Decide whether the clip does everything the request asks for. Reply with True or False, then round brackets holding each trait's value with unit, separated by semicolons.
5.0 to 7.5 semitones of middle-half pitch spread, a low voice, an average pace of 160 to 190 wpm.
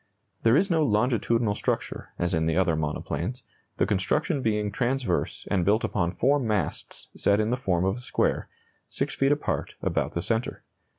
True (5.5 semitones; 110 Hz; 175 wpm)